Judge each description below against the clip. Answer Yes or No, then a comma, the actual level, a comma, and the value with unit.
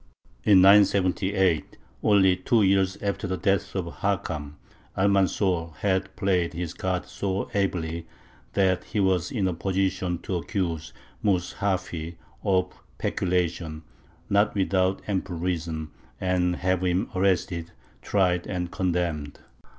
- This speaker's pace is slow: Yes, slow, 120 wpm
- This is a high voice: No, very low, 95 Hz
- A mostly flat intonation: Yes, narrow, 2.0 semitones